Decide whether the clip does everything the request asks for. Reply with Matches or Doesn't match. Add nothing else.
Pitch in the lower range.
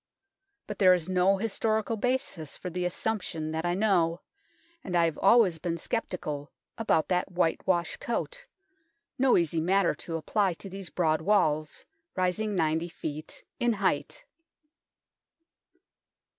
Doesn't match